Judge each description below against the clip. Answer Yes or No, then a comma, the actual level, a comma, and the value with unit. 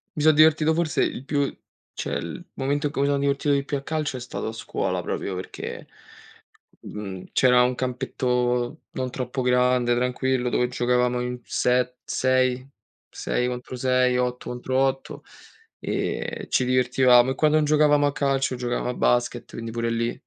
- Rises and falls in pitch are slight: Yes, narrow, 2.0 semitones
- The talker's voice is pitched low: Yes, low, 125 Hz